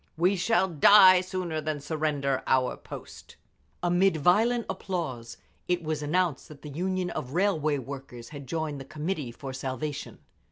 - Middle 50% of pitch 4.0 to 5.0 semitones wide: Yes, average, 4.6 semitones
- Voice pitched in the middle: Yes, medium, 155 Hz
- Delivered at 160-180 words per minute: No, average, 150 wpm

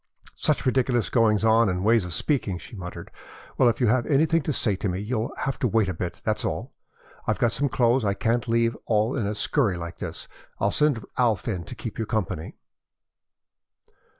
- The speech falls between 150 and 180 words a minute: No, average, 200 wpm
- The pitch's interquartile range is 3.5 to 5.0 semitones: Yes, average, 3.8 semitones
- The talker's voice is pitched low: Yes, low, 115 Hz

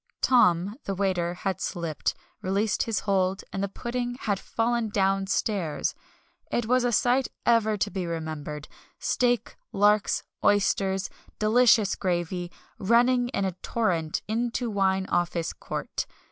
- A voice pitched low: No, high, 200 Hz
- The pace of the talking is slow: Yes, slow, 130 wpm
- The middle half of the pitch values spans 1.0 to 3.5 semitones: No, average, 4.0 semitones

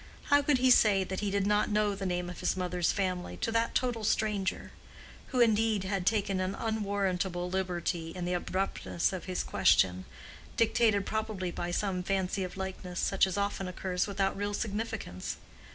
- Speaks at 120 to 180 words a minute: Yes, average, 170 wpm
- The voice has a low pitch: No, high, 195 Hz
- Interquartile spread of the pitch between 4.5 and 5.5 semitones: No, narrow, 2.6 semitones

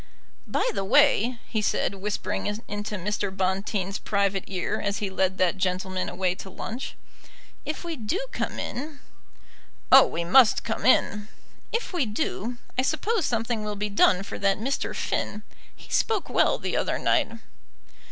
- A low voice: No, high, 210 Hz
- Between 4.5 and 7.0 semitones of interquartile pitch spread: No, average, 4.1 semitones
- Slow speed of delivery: No, average, 160 wpm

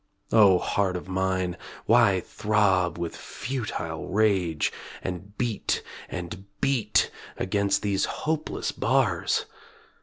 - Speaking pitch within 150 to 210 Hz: No, very low, 95 Hz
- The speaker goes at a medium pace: No, slow, 100 wpm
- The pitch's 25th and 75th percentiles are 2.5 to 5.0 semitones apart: Yes, average, 2.9 semitones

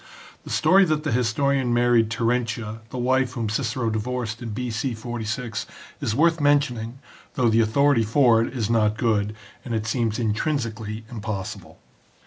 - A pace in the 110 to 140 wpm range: No, average, 150 wpm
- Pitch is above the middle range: No, low, 115 Hz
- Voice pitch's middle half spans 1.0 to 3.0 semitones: Yes, narrow, 2.6 semitones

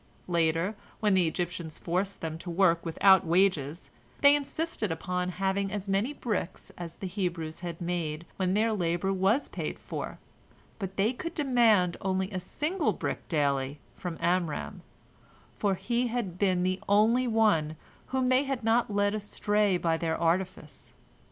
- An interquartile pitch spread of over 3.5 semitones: Yes, average, 3.9 semitones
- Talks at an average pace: Yes, average, 155 wpm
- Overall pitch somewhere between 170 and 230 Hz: Yes, high, 190 Hz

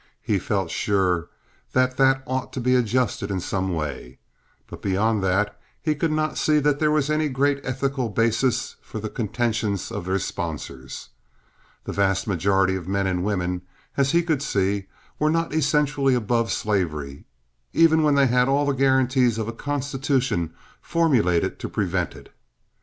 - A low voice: Yes, low, 120 Hz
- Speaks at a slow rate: No, average, 165 wpm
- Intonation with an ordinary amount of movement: No, wide, 6.3 semitones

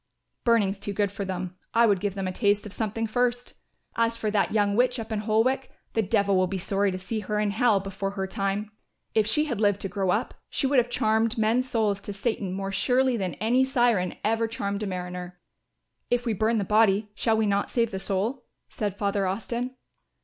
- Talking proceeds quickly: Yes, fast, 215 wpm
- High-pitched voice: Yes, high, 210 Hz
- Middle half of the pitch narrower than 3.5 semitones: Yes, average, 2.8 semitones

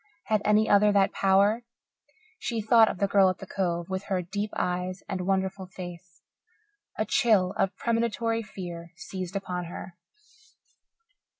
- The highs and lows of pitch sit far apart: No, narrow, 2.5 semitones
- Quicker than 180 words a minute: No, average, 145 wpm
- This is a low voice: No, high, 195 Hz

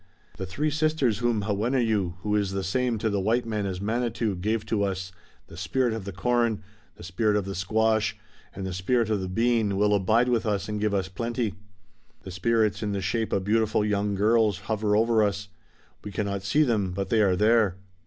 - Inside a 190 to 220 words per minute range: Yes, fast, 205 wpm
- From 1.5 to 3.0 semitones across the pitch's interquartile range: Yes, average, 2.7 semitones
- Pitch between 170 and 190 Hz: No, low, 105 Hz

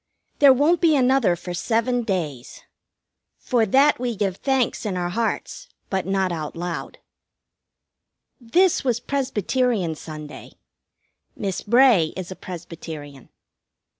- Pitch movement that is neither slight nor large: No, wide, 6.6 semitones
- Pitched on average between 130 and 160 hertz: No, high, 205 Hz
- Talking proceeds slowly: Yes, slow, 120 wpm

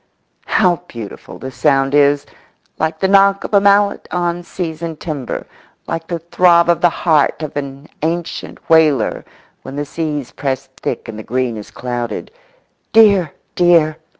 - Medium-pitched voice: Yes, medium, 160 Hz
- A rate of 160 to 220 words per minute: No, average, 150 wpm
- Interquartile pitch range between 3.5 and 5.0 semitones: Yes, average, 4.1 semitones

